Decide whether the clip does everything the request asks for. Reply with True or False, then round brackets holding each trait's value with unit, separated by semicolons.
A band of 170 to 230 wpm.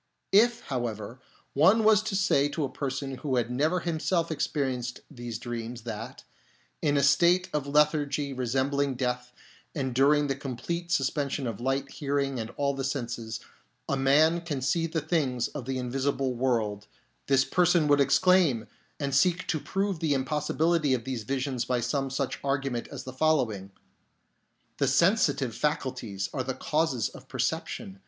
False (160 wpm)